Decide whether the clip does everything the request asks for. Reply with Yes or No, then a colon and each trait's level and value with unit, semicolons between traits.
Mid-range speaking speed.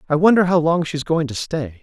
No: fast, 265 wpm